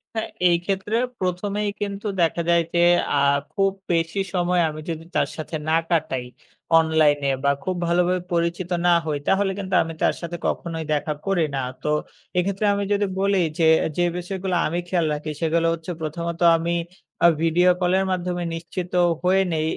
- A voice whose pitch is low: No, medium, 175 Hz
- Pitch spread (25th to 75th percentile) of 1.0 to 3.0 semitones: Yes, narrow, 2.5 semitones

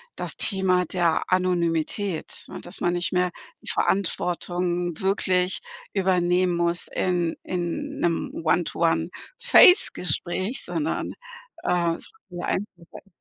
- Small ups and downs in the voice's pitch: Yes, narrow, 1.6 semitones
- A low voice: No, medium, 180 Hz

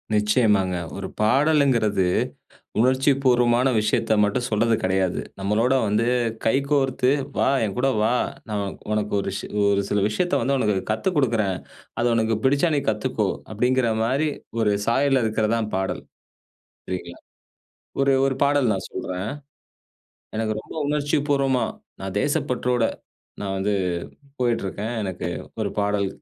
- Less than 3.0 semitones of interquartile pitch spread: No, average, 4.3 semitones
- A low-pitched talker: Yes, low, 115 Hz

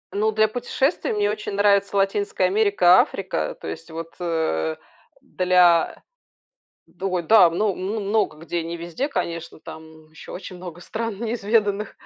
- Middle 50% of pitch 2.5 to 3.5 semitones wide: No, average, 3.9 semitones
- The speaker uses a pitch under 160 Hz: No, high, 190 Hz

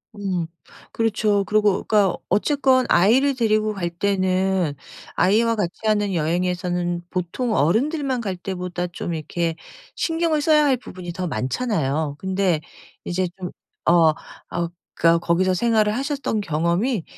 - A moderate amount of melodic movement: Yes, average, 4.4 semitones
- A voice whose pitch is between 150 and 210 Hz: Yes, high, 190 Hz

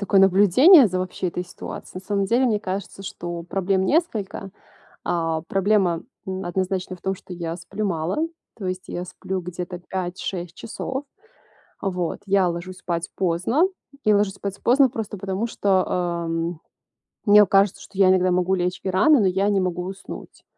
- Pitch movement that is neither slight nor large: No, narrow, 2.1 semitones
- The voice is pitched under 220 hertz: Yes, high, 190 Hz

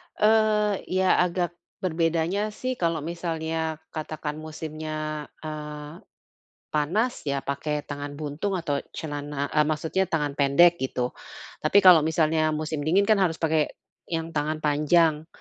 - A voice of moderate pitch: Yes, medium, 155 Hz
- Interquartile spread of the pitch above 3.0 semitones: No, narrow, 2.5 semitones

